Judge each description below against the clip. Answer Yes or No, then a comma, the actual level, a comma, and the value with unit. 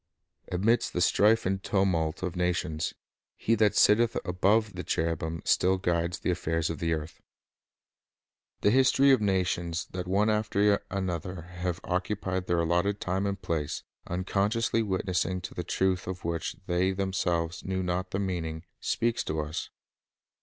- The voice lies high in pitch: No, very low, 90 Hz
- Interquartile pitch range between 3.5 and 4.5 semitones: No, average, 2.7 semitones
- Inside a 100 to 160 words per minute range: Yes, average, 150 wpm